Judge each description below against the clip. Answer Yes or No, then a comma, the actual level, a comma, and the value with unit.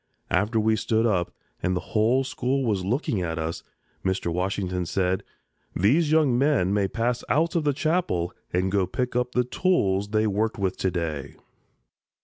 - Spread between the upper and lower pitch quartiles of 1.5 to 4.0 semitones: No, average, 5.2 semitones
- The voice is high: No, low, 105 Hz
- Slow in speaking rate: No, average, 175 wpm